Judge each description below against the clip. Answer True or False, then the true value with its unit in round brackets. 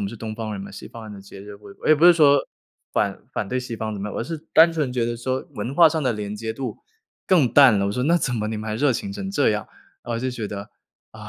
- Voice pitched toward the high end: False (115 Hz)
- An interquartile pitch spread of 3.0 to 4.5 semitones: False (5.1 semitones)